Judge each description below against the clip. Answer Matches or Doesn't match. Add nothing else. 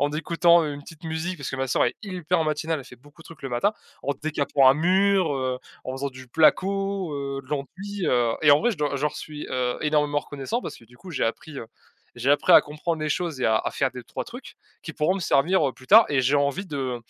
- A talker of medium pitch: Matches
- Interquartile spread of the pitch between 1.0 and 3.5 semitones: Doesn't match